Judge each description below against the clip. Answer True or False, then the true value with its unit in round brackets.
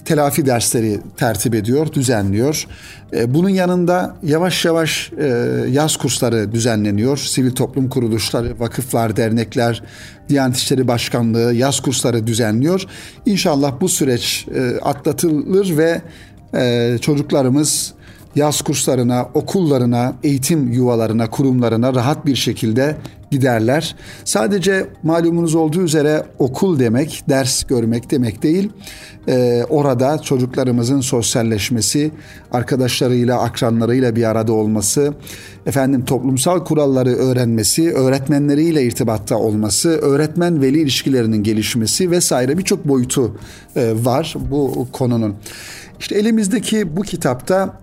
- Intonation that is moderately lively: True (4.7 semitones)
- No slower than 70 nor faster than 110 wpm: True (100 wpm)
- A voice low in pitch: True (130 Hz)